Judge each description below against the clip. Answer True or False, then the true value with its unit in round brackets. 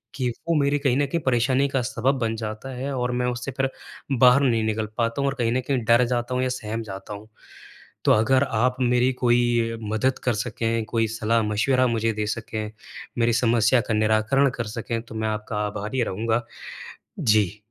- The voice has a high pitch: False (120 Hz)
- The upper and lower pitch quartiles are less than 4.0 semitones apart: True (2.6 semitones)